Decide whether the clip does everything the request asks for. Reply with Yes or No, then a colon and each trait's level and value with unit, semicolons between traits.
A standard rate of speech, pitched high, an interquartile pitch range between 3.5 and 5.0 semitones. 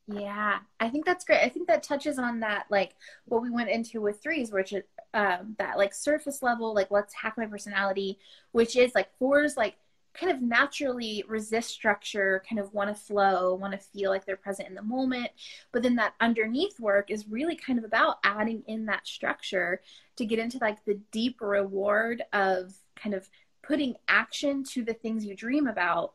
Yes: average, 195 wpm; high, 220 Hz; average, 4.0 semitones